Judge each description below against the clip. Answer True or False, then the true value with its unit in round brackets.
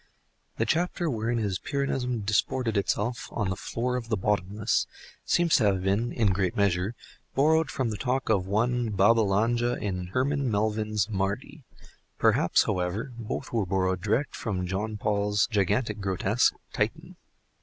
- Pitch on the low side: True (110 Hz)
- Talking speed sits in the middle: True (145 wpm)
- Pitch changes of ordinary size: True (3.8 semitones)